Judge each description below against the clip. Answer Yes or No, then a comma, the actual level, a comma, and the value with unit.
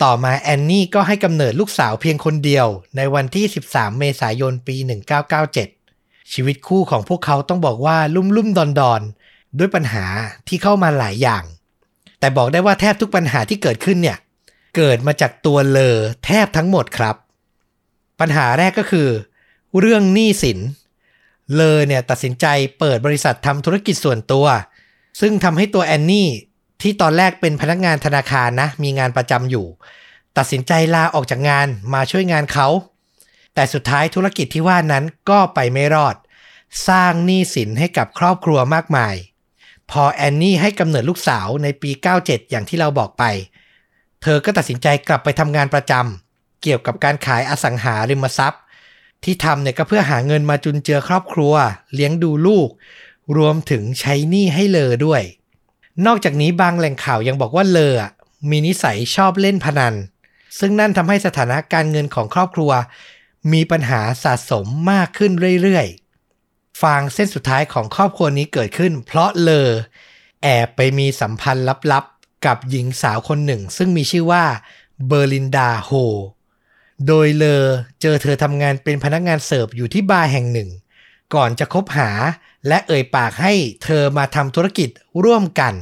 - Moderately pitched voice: Yes, medium, 145 Hz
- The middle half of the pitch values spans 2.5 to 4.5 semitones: No, average, 4.9 semitones